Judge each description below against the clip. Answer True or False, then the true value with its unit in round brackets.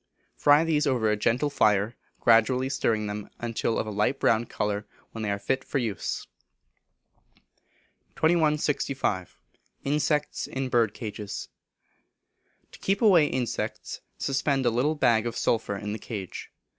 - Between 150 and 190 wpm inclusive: False (135 wpm)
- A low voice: True (120 Hz)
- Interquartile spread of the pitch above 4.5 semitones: True (5.1 semitones)